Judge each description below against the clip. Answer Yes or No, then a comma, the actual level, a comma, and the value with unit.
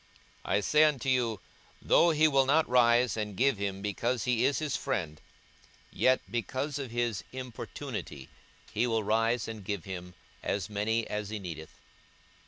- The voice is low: Yes, low, 115 Hz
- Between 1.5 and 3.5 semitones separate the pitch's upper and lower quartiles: No, average, 4.1 semitones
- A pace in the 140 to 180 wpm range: Yes, average, 165 wpm